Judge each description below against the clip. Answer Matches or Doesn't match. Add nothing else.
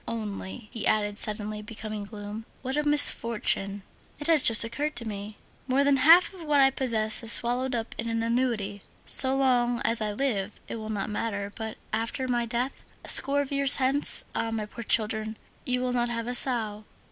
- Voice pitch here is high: Matches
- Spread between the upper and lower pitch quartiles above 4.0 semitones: Doesn't match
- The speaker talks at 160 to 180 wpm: Doesn't match